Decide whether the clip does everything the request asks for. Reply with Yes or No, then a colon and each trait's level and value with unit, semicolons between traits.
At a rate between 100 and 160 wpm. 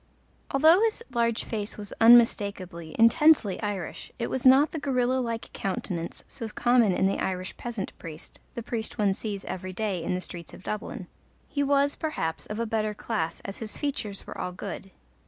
No: average, 180 wpm